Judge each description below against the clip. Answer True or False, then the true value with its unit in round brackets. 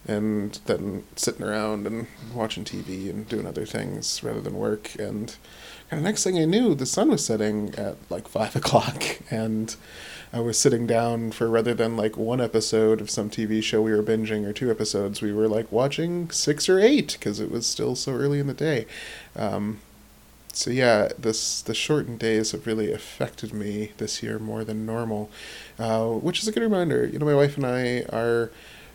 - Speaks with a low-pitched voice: True (115 Hz)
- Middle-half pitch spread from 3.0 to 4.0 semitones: False (2.5 semitones)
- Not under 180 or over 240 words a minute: True (195 wpm)